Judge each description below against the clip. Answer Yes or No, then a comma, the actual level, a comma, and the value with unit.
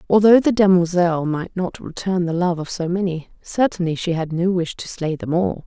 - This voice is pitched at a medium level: Yes, medium, 175 Hz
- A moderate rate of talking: No, fast, 210 wpm